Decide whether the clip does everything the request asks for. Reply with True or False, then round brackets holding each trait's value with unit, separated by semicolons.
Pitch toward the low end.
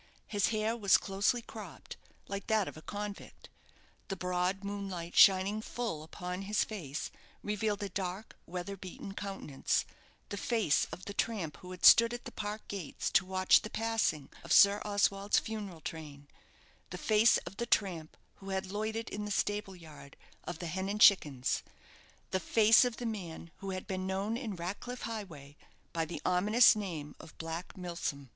False (195 Hz)